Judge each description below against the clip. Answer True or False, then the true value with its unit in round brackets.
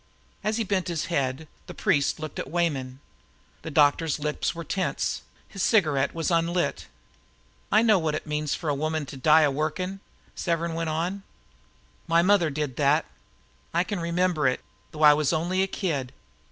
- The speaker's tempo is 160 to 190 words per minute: True (175 wpm)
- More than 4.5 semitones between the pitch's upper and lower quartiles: False (3.1 semitones)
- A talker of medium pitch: True (160 Hz)